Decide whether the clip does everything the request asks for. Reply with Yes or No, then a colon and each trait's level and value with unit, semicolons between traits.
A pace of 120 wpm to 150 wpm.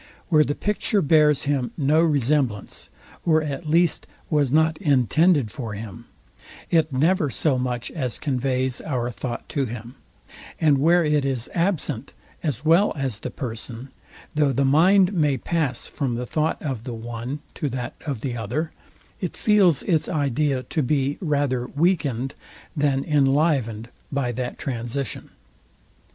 Yes: average, 145 wpm